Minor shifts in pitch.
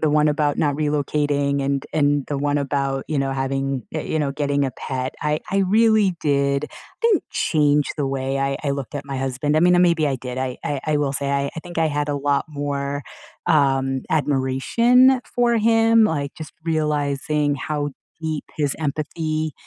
Yes: narrow, 2.1 semitones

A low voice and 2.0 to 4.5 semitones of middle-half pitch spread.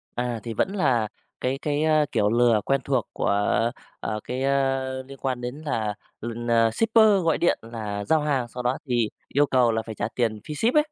Yes: low, 125 Hz; average, 4.0 semitones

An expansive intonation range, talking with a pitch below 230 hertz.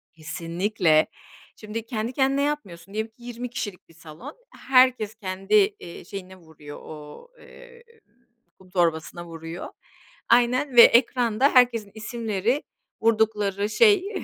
Yes: wide, 5.7 semitones; high, 215 Hz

